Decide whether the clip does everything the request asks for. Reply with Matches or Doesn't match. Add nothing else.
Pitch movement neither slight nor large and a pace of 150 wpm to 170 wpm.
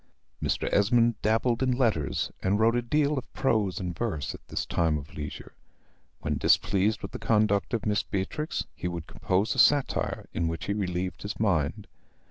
Doesn't match